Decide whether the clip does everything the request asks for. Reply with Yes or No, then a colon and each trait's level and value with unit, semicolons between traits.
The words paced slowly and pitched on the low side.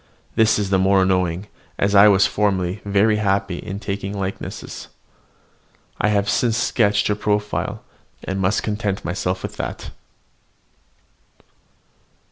Yes: slow, 125 wpm; low, 100 Hz